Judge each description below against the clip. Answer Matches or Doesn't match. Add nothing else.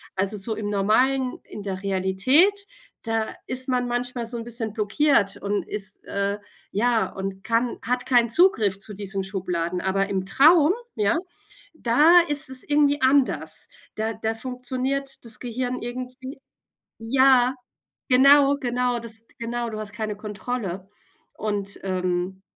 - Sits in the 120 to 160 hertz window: Doesn't match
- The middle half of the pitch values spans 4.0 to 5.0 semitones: Matches